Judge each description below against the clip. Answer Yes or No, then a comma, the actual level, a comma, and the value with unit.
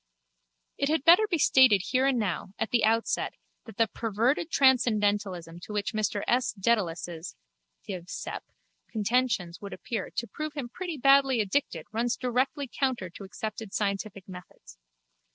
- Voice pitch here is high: Yes, high, 225 Hz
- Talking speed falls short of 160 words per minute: Yes, average, 150 wpm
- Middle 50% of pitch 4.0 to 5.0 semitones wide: Yes, average, 4.7 semitones